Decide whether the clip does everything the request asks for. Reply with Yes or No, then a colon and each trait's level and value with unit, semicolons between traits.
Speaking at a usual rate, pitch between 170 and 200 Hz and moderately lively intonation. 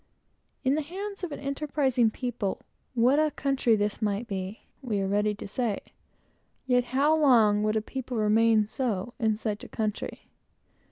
No: average, 165 wpm; high, 230 Hz; average, 4.3 semitones